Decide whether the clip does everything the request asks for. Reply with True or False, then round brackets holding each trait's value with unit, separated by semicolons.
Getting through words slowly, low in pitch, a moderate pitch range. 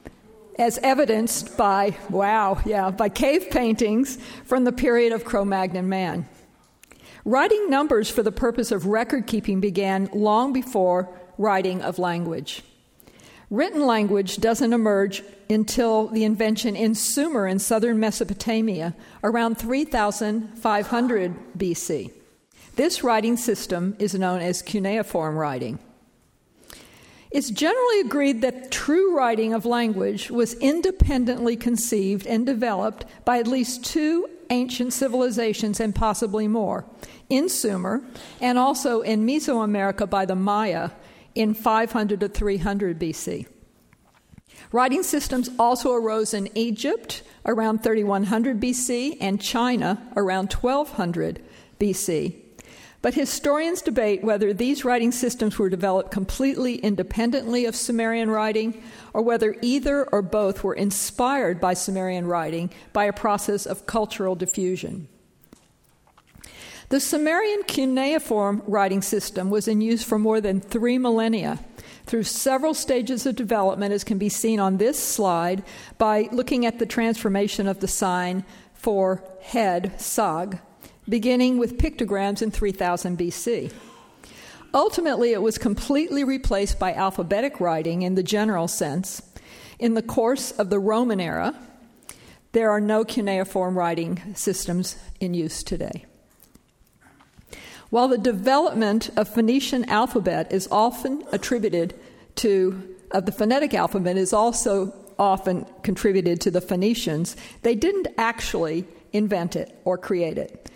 False (125 wpm; 220 Hz; 3.8 semitones)